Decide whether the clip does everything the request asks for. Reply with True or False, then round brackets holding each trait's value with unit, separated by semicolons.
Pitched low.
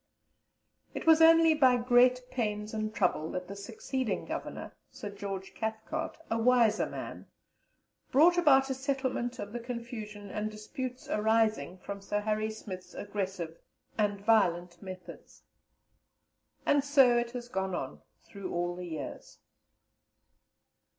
False (220 Hz)